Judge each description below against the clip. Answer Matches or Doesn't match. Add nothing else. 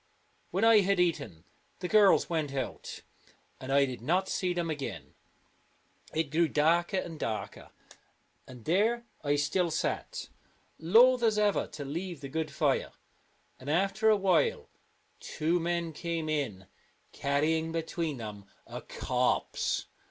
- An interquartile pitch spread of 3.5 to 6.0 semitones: Matches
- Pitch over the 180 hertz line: Doesn't match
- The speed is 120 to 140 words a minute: Matches